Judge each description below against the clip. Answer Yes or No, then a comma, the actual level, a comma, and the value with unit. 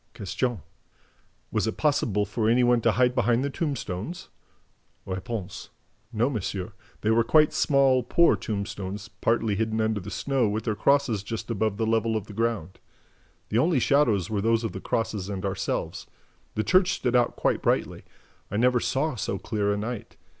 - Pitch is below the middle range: Yes, low, 110 Hz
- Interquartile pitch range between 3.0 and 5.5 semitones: Yes, average, 3.4 semitones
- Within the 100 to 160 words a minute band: No, average, 175 wpm